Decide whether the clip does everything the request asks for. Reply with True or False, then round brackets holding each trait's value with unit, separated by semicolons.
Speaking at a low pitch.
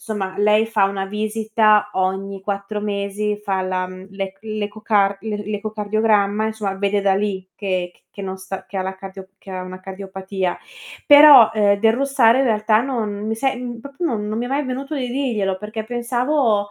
False (210 Hz)